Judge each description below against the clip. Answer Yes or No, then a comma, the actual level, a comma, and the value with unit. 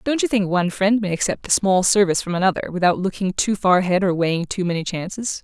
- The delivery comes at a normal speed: No, fast, 245 wpm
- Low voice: No, high, 190 Hz